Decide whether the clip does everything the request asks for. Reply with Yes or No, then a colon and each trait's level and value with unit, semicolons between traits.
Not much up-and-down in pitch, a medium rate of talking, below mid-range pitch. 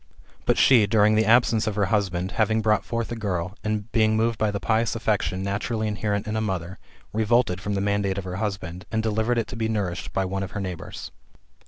No: narrow, 2.3 semitones; fast, 220 wpm; low, 105 Hz